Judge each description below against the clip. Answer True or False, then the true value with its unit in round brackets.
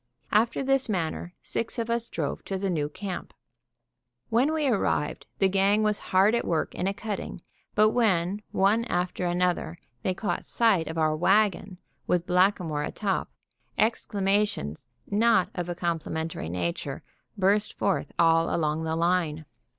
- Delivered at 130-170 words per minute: True (150 wpm)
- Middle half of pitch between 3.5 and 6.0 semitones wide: True (4.2 semitones)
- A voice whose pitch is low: False (185 Hz)